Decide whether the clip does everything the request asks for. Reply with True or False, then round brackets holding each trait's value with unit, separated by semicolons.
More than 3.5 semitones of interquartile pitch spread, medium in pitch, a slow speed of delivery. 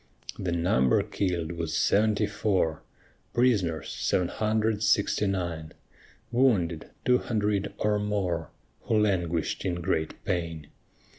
False (4.2 semitones; 95 Hz; 115 wpm)